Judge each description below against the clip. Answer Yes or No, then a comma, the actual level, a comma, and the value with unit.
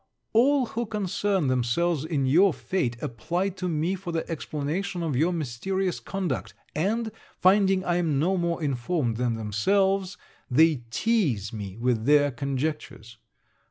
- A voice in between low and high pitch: Yes, medium, 165 Hz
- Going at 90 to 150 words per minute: Yes, average, 140 wpm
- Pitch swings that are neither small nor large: No, wide, 6.8 semitones